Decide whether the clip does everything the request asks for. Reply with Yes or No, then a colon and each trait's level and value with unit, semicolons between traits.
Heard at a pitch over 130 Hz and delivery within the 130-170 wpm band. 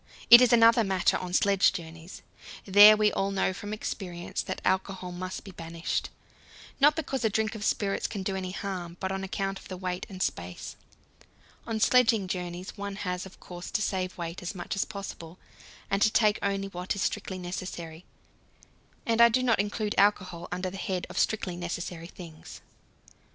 No: high, 190 Hz; average, 180 wpm